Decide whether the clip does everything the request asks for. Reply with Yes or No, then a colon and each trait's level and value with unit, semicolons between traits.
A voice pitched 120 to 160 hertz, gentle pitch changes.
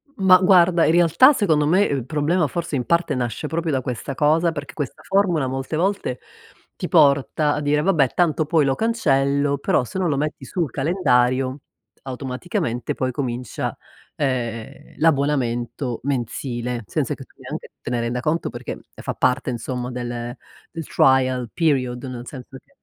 No: medium, 140 Hz; average, 4.5 semitones